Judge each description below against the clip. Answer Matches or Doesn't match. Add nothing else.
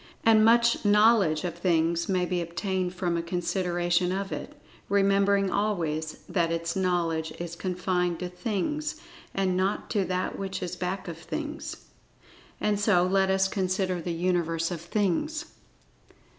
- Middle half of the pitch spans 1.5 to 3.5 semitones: Matches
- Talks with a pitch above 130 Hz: Matches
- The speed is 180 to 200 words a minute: Doesn't match